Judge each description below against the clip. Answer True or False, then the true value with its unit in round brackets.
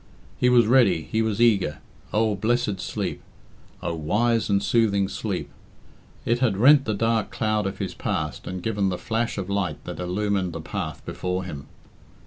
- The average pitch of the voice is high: False (105 Hz)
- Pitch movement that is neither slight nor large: True (3.6 semitones)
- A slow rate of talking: False (175 wpm)